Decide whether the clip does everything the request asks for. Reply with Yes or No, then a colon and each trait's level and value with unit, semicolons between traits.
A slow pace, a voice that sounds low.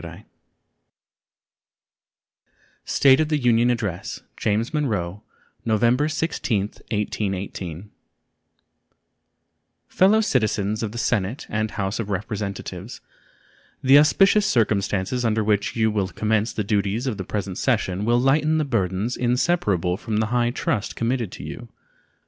Yes: slow, 120 wpm; low, 110 Hz